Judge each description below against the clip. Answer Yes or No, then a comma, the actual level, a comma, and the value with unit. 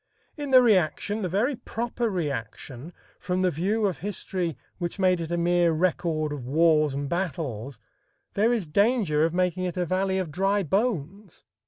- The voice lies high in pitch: No, medium, 180 Hz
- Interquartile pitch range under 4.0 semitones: No, average, 4.3 semitones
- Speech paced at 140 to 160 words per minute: No, average, 170 wpm